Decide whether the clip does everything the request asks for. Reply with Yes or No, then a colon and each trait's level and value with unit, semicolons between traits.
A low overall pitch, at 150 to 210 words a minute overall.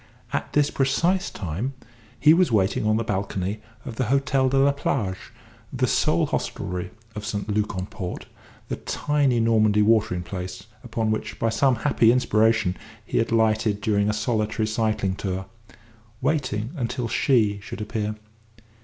Yes: low, 110 Hz; average, 155 wpm